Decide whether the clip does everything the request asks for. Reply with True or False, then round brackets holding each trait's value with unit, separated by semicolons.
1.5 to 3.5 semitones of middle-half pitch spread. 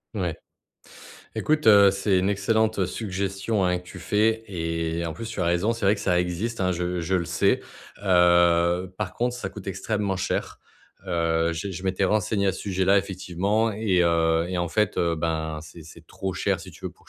True (2.8 semitones)